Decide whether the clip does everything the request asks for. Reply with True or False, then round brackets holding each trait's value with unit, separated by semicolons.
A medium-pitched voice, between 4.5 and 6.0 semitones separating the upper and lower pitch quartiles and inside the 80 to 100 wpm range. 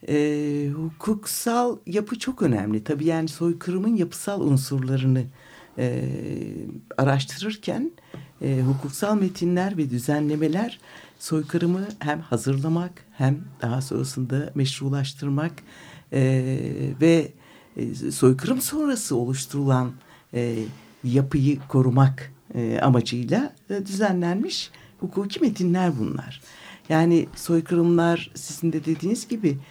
True (150 Hz; 4.9 semitones; 95 wpm)